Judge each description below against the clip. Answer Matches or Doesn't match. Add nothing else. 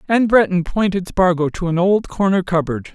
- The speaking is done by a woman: Doesn't match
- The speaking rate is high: Doesn't match